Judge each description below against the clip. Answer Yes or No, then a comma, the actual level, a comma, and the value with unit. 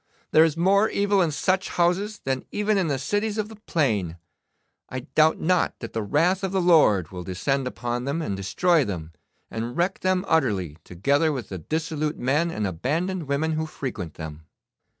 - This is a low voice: No, medium, 150 Hz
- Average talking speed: Yes, average, 185 wpm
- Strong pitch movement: Yes, wide, 8.1 semitones